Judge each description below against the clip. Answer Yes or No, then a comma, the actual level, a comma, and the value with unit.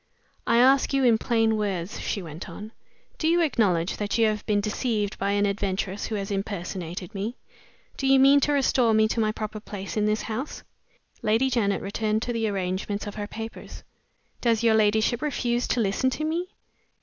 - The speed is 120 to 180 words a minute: No, average, 190 wpm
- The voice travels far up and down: No, average, 2.9 semitones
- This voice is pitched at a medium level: No, high, 215 Hz